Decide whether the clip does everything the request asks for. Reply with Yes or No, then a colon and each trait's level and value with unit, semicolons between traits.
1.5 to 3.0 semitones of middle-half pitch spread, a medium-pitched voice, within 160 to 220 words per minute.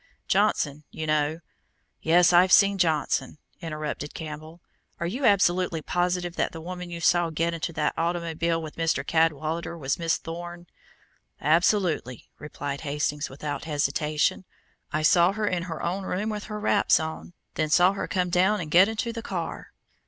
Yes: average, 2.7 semitones; medium, 170 Hz; average, 165 wpm